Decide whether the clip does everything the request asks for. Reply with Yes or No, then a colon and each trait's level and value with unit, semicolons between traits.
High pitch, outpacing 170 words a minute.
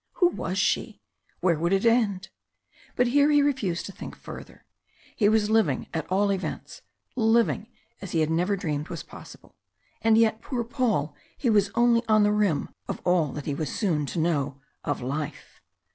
Yes: high, 200 Hz; average, 180 wpm